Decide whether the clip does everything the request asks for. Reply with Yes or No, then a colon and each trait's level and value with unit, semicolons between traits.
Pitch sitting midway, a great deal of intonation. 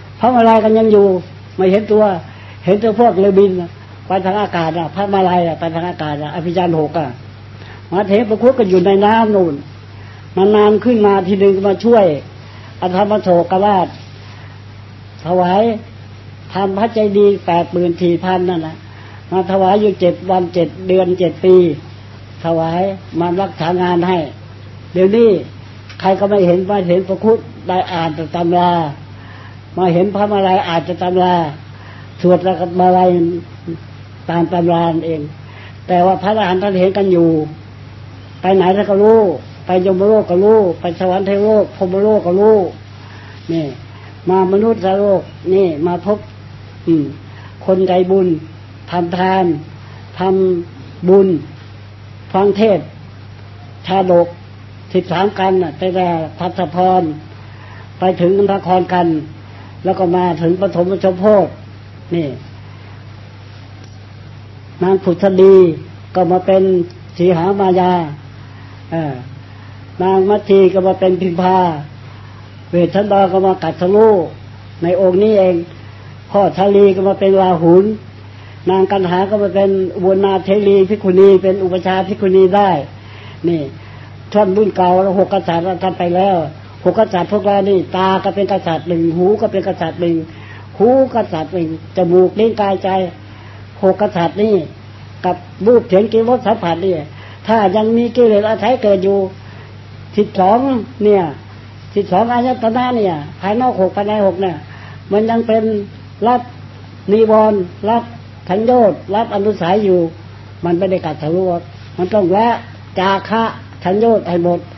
Yes: medium, 180 Hz; wide, 8.4 semitones